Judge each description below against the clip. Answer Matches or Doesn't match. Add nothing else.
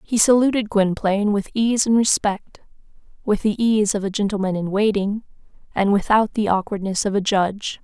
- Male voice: Doesn't match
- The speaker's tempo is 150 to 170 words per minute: Matches